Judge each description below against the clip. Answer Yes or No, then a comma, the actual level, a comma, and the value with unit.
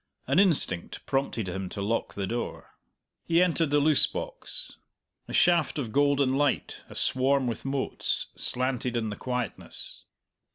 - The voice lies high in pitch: No, low, 135 Hz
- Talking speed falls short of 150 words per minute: Yes, average, 140 wpm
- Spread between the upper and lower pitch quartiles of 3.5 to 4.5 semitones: Yes, average, 4.1 semitones